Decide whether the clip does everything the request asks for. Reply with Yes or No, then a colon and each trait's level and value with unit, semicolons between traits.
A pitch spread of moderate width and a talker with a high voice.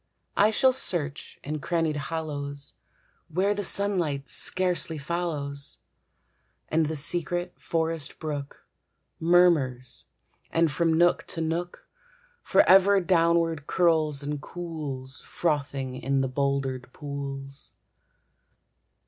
No: average, 3.6 semitones; medium, 155 Hz